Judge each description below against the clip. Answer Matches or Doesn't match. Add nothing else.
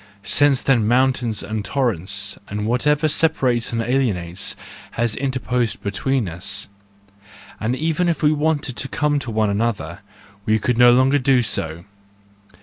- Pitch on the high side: Doesn't match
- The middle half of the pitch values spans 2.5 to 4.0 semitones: Doesn't match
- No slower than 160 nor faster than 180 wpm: Doesn't match